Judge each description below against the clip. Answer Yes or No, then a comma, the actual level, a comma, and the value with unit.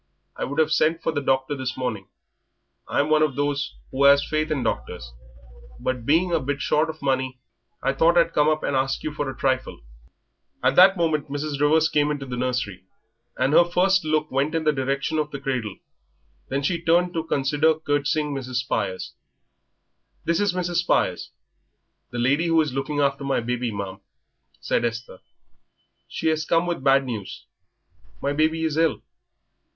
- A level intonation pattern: No, average, 3.2 semitones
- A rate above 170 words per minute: Yes, average, 180 wpm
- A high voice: No, medium, 145 Hz